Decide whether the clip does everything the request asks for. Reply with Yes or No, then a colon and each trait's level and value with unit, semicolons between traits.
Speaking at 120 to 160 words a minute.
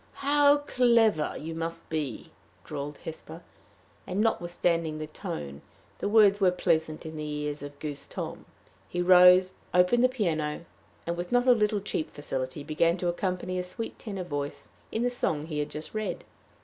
No: average, 170 wpm